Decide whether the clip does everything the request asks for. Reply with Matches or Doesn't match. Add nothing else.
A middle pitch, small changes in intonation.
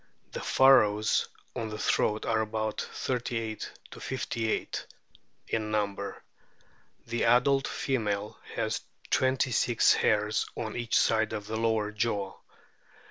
Doesn't match